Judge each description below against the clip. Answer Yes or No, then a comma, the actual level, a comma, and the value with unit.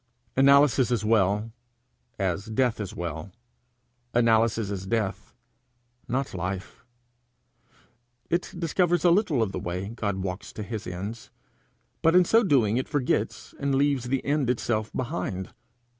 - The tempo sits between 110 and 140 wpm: Yes, slow, 135 wpm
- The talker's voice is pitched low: Yes, low, 115 Hz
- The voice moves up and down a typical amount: No, wide, 5.9 semitones